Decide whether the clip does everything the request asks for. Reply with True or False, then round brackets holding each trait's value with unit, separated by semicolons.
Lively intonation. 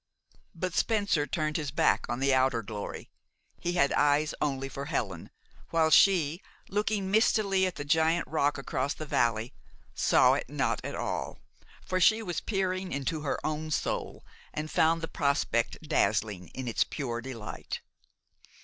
False (4.9 semitones)